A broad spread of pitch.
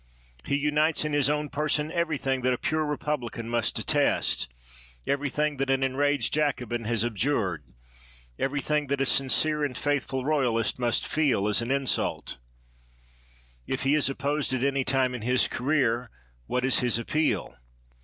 No: average, 3.0 semitones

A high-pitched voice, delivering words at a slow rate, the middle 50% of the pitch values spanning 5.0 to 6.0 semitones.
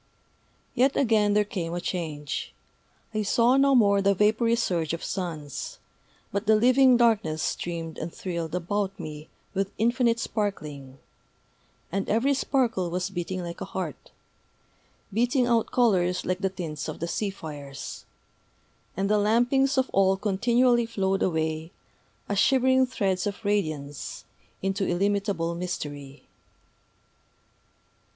Yes: high, 195 Hz; slow, 130 wpm; average, 5.3 semitones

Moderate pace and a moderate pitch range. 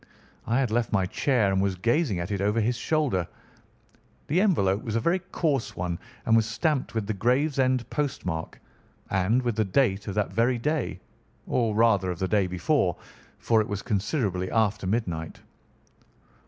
Yes: average, 170 wpm; average, 4.9 semitones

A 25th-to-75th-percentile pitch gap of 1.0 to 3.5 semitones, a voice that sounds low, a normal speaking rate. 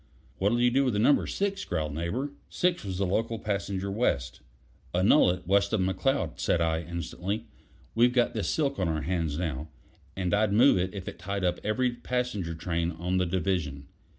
No: wide, 5.4 semitones; very low, 95 Hz; average, 185 wpm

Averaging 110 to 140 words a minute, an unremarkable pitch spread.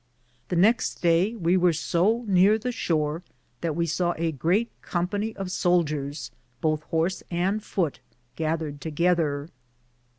Yes: slow, 135 wpm; average, 3.2 semitones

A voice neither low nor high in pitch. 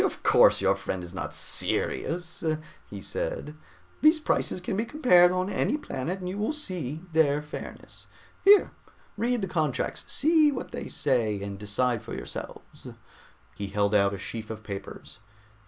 Yes: medium, 155 Hz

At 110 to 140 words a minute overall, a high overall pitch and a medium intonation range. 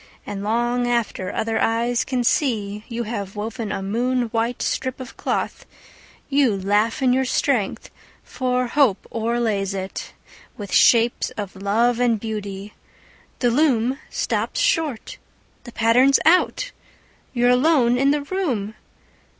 Yes: slow, 135 wpm; high, 235 Hz; average, 3.3 semitones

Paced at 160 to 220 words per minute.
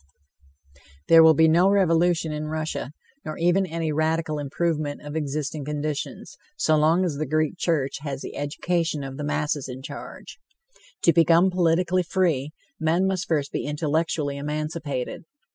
No: average, 150 wpm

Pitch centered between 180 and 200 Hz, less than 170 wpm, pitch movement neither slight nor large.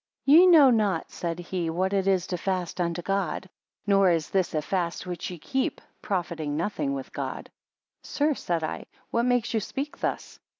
No: medium, 185 Hz; average, 185 wpm; average, 4.0 semitones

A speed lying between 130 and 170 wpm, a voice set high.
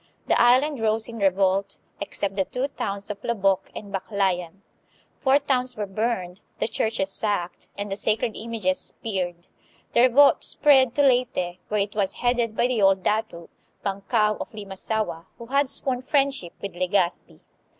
Yes: average, 160 wpm; high, 210 Hz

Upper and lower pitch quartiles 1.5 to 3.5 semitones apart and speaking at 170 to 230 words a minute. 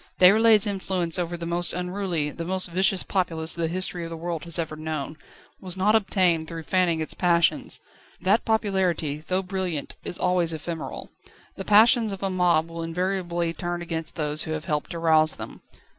Yes: narrow, 2.5 semitones; average, 180 wpm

